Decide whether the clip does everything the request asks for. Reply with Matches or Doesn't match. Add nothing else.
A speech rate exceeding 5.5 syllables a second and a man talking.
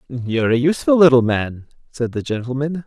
Matches